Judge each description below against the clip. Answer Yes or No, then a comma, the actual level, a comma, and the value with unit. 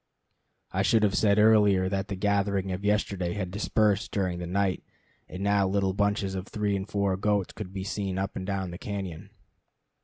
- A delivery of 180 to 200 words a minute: Yes, average, 190 wpm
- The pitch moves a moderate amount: No, narrow, 1.4 semitones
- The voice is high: No, low, 100 Hz